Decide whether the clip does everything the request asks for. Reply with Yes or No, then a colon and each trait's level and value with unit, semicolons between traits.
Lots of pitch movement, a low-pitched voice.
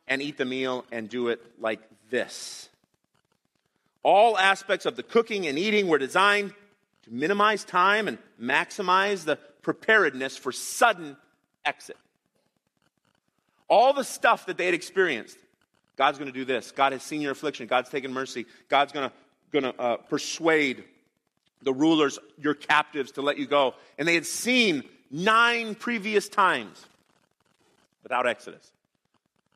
No: wide, 7.1 semitones; medium, 150 Hz